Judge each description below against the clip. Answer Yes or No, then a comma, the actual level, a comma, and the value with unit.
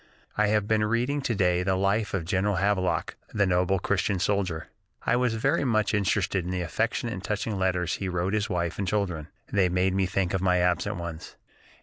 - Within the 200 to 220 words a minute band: Yes, fast, 205 wpm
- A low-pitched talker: Yes, very low, 95 Hz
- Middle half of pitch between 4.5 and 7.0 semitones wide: No, average, 2.8 semitones